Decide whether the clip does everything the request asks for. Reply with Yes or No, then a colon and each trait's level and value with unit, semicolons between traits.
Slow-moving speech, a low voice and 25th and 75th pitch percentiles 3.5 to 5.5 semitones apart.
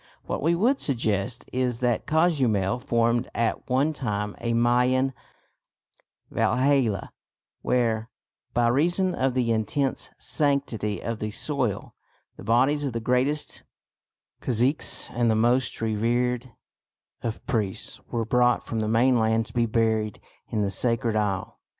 No: slow, 130 wpm; low, 120 Hz; average, 2.8 semitones